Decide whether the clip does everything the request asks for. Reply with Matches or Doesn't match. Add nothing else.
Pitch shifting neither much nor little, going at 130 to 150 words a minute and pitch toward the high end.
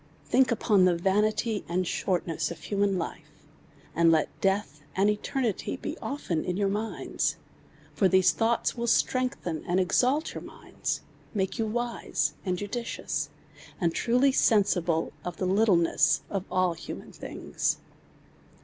Matches